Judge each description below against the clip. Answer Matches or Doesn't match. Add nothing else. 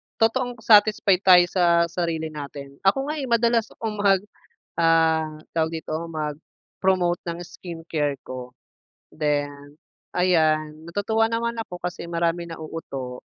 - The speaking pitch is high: Doesn't match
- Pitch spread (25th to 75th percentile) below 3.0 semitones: Doesn't match